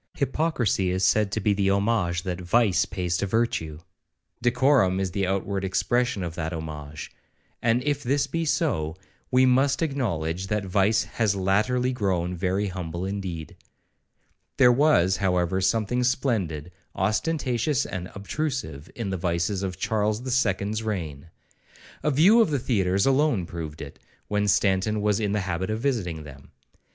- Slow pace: No, average, 150 wpm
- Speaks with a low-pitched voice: Yes, low, 100 Hz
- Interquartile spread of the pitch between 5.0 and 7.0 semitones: Yes, average, 5.3 semitones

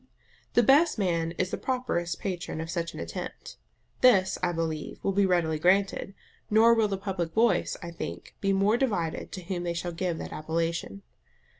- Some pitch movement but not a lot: Yes, average, 3.3 semitones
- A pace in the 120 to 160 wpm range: No, average, 180 wpm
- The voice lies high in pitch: No, medium, 180 Hz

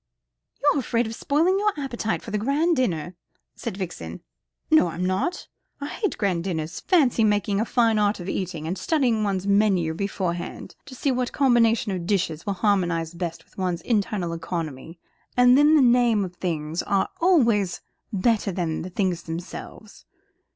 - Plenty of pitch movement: Yes, wide, 5.7 semitones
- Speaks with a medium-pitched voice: No, high, 200 Hz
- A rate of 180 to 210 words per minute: No, average, 170 wpm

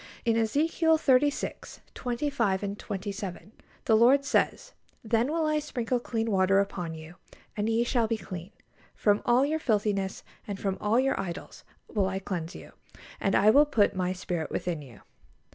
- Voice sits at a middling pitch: No, high, 215 Hz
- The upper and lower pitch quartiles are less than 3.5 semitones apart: No, average, 4.6 semitones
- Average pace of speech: Yes, average, 165 wpm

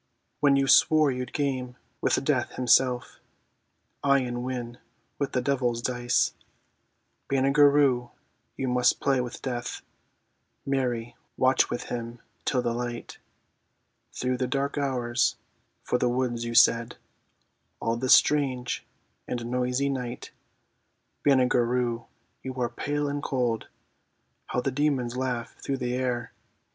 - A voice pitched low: Yes, low, 125 Hz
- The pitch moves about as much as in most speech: No, narrow, 1.9 semitones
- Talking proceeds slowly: Yes, slow, 130 wpm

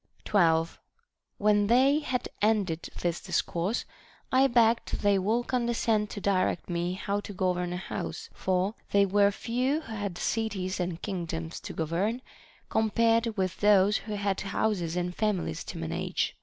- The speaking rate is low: No, average, 155 wpm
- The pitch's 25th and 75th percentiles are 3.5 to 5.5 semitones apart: Yes, average, 3.8 semitones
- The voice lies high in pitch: Yes, high, 200 Hz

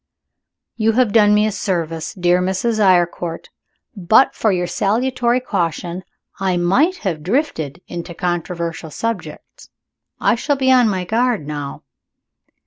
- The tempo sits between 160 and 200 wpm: No, slow, 135 wpm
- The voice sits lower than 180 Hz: No, high, 190 Hz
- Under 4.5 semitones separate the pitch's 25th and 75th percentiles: No, average, 4.9 semitones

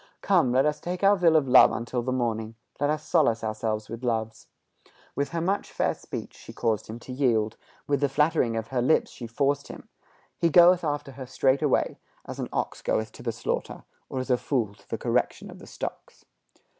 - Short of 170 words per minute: No, fast, 205 wpm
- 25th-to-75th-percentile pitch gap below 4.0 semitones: No, average, 4.5 semitones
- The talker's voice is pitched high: No, low, 130 Hz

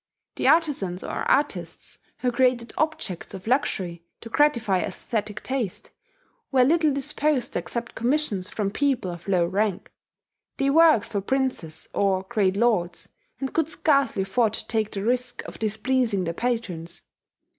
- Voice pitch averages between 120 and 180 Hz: No, high, 230 Hz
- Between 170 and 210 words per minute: No, average, 145 wpm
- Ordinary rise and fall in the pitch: No, wide, 5.7 semitones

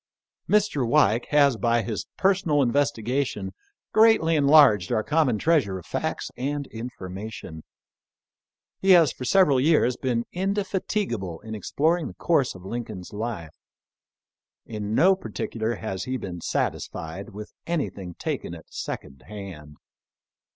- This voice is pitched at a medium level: No, low, 120 Hz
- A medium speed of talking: No, slow, 130 wpm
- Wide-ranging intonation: Yes, wide, 6.8 semitones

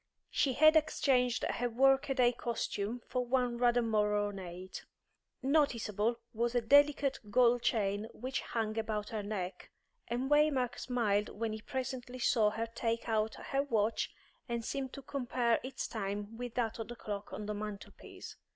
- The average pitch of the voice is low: No, high, 235 Hz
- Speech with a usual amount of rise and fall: Yes, average, 3.1 semitones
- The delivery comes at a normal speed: Yes, average, 160 wpm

